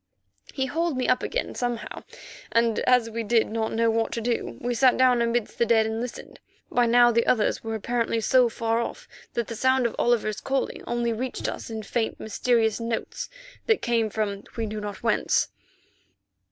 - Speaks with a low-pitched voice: No, high, 235 Hz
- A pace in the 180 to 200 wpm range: Yes, average, 190 wpm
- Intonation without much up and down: Yes, narrow, 1.6 semitones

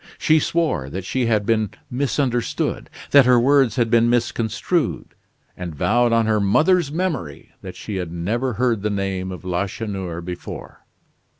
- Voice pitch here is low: Yes, low, 115 Hz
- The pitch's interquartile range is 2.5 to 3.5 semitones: No, average, 4.9 semitones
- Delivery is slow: No, average, 155 wpm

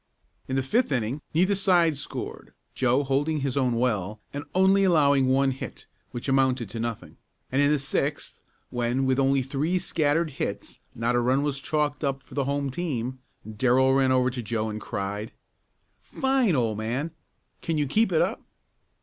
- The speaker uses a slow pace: No, average, 175 wpm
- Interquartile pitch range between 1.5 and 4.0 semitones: Yes, average, 3.3 semitones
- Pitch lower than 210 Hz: Yes, low, 135 Hz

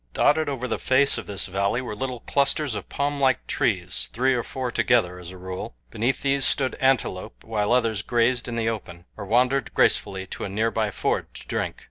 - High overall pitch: No, low, 115 Hz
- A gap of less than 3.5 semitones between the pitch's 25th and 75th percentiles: No, average, 4.4 semitones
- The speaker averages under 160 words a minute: No, average, 195 wpm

